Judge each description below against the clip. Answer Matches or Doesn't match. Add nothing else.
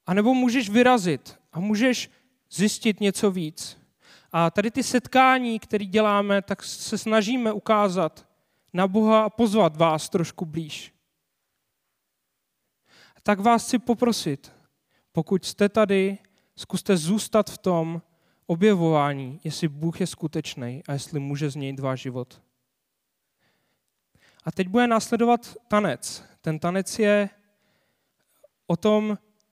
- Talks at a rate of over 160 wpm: Doesn't match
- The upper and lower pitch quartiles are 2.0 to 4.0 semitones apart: Doesn't match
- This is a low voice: Doesn't match